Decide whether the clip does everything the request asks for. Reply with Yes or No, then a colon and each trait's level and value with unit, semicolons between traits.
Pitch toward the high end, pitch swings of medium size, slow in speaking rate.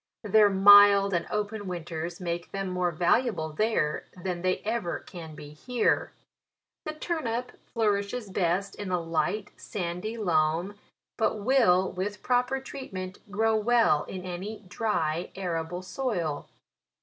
Yes: high, 195 Hz; average, 4.0 semitones; slow, 130 wpm